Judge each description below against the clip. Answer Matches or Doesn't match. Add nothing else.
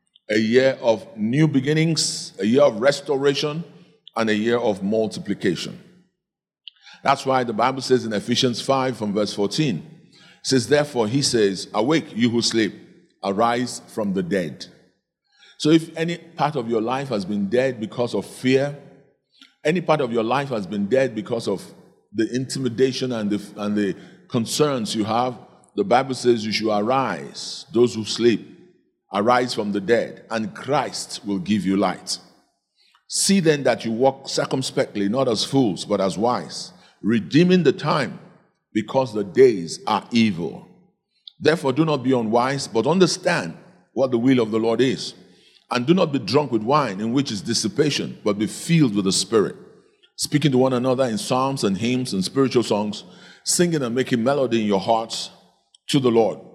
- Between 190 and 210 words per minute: Doesn't match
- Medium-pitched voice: Doesn't match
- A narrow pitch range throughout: Doesn't match